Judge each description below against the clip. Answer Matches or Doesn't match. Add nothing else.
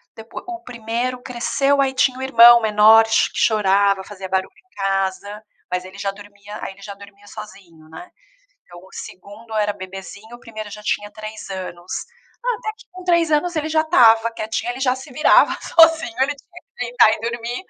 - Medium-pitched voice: Doesn't match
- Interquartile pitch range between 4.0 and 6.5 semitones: Matches